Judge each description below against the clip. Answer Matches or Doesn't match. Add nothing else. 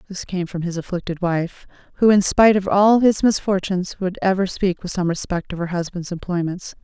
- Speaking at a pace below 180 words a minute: Doesn't match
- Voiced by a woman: Matches